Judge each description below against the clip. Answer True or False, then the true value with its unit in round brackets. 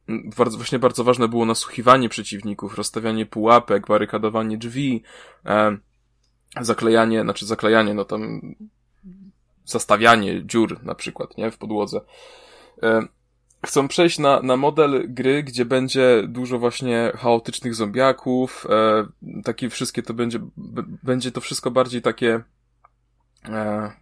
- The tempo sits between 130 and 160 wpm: False (120 wpm)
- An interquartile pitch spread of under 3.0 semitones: True (2.5 semitones)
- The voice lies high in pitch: False (120 Hz)